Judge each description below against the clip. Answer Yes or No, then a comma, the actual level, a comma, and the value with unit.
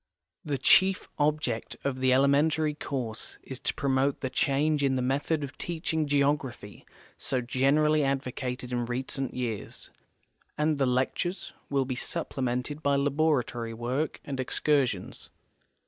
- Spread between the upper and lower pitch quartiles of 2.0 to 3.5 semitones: Yes, average, 2.7 semitones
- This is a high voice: No, low, 135 Hz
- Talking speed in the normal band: No, slow, 130 wpm